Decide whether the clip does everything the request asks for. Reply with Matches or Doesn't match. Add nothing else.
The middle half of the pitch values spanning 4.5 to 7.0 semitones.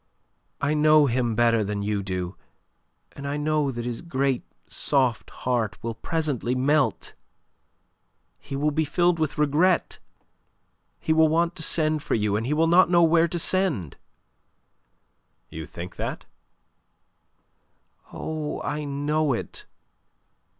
Matches